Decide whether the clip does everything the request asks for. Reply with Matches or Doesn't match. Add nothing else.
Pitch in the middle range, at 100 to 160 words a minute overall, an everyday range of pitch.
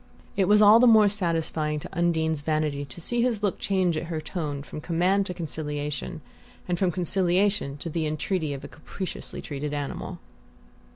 Doesn't match